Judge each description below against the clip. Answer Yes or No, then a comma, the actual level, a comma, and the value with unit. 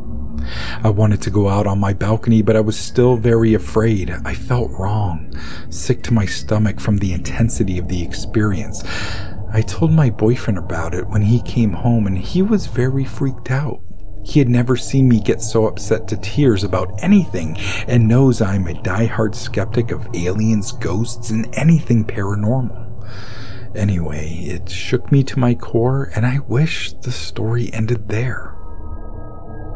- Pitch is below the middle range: Yes, low, 110 Hz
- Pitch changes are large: No, average, 3.4 semitones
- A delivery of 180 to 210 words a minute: No, average, 165 wpm